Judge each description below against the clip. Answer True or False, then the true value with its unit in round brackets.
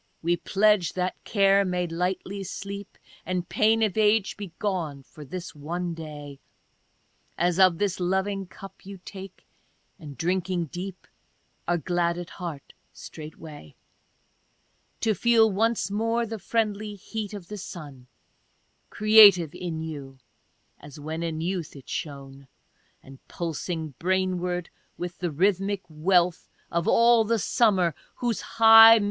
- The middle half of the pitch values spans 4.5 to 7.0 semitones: False (3.7 semitones)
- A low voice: False (180 Hz)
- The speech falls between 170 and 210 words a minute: False (135 wpm)